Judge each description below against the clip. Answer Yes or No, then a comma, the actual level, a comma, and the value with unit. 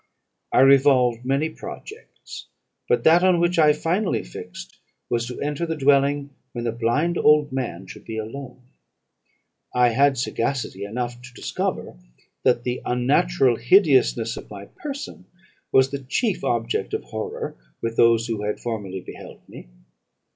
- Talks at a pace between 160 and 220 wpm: No, average, 145 wpm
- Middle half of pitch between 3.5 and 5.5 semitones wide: Yes, average, 4.6 semitones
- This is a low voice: Yes, low, 130 Hz